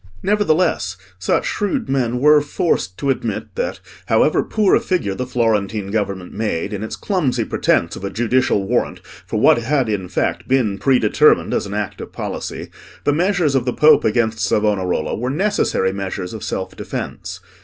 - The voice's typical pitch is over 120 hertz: No, low, 115 Hz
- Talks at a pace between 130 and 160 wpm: No, average, 170 wpm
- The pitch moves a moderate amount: No, wide, 6.5 semitones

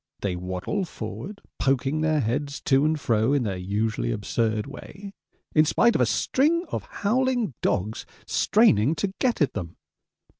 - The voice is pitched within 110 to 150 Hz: Yes, medium, 140 Hz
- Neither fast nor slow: Yes, average, 155 wpm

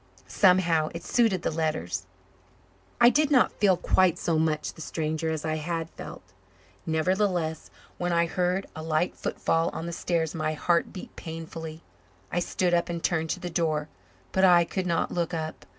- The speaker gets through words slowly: No, average, 175 wpm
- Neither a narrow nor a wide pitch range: No, narrow, 2.1 semitones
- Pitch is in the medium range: Yes, medium, 165 Hz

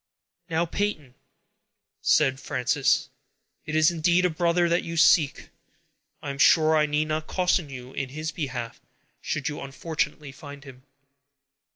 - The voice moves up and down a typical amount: Yes, average, 3.2 semitones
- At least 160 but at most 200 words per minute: No, average, 145 wpm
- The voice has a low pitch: No, medium, 155 Hz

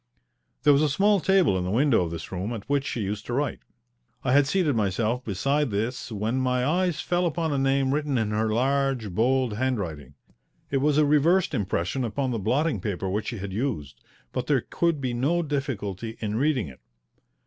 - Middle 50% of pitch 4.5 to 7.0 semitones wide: Yes, wide, 5.4 semitones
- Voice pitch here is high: No, low, 125 Hz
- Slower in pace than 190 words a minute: No, fast, 205 wpm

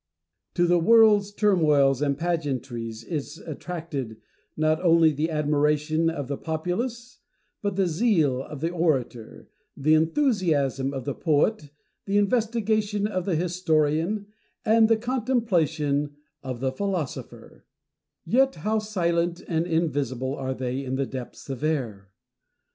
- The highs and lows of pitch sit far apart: Yes, wide, 5.9 semitones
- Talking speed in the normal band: No, slow, 130 wpm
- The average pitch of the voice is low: No, medium, 160 Hz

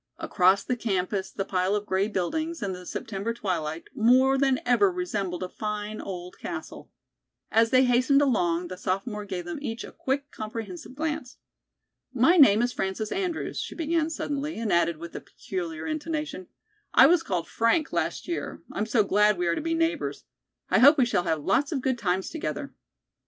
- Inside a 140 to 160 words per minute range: No, average, 185 wpm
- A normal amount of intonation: No, wide, 6.9 semitones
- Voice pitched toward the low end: No, high, 220 Hz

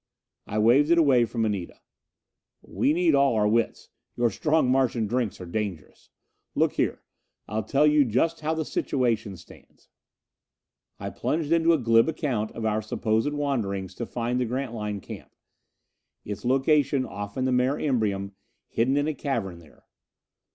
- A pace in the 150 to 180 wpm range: Yes, average, 160 wpm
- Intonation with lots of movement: No, average, 5.0 semitones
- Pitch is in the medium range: No, low, 120 Hz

